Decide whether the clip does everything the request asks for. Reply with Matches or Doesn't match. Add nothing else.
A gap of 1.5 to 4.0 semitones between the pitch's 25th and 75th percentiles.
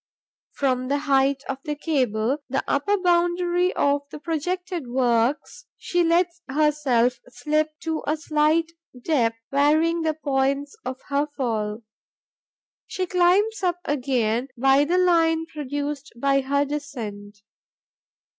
Matches